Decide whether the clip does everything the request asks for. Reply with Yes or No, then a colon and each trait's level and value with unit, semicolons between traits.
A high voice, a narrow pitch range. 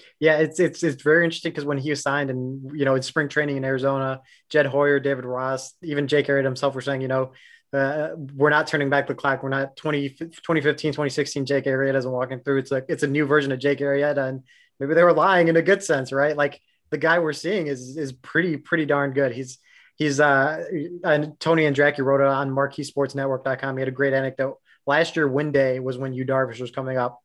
No: medium, 140 Hz; narrow, 2.0 semitones